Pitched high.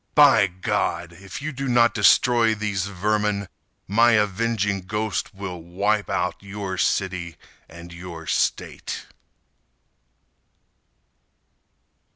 No: low, 100 Hz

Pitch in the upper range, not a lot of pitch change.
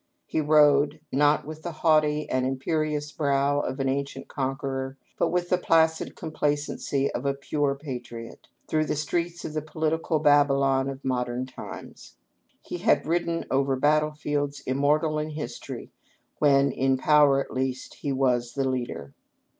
No: medium, 145 Hz; narrow, 2.3 semitones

